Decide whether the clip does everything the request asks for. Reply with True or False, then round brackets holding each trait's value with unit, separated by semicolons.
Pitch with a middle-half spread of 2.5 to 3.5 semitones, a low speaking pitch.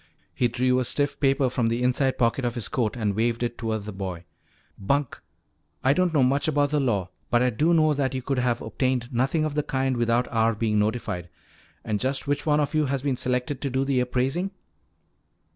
True (3.1 semitones; 125 Hz)